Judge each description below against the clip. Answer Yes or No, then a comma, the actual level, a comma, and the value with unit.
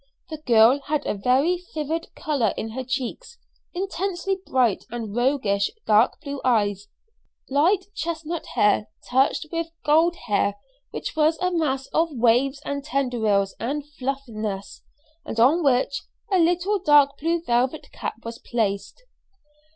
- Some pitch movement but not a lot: No, wide, 6.0 semitones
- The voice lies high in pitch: Yes, very high, 275 Hz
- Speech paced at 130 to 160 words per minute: Yes, slow, 135 wpm